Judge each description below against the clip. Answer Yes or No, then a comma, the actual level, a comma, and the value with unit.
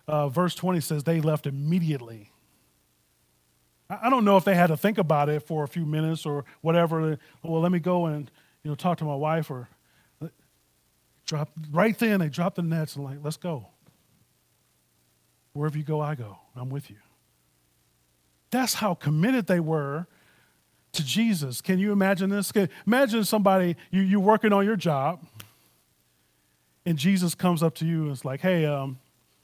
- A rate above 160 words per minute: Yes, average, 175 wpm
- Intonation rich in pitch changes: Yes, wide, 7.0 semitones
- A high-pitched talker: No, medium, 155 Hz